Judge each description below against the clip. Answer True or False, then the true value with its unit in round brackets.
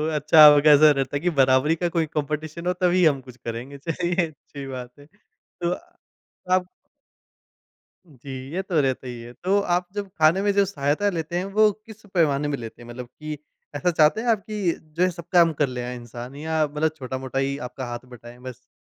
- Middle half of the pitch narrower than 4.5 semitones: False (5.0 semitones)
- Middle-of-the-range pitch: True (150 Hz)